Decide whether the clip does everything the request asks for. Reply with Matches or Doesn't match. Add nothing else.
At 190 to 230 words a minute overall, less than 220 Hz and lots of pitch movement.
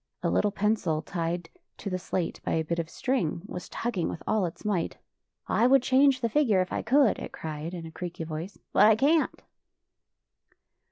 Matches